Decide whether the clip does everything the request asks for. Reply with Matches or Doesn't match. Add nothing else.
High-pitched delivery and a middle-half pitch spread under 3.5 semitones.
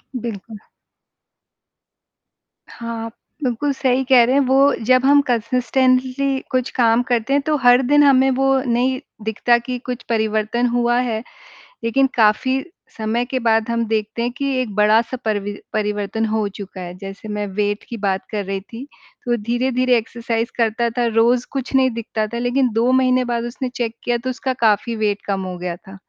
Matches